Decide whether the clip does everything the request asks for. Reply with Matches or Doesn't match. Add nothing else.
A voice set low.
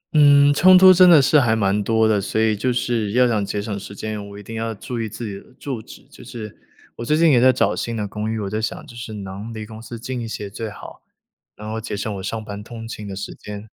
Matches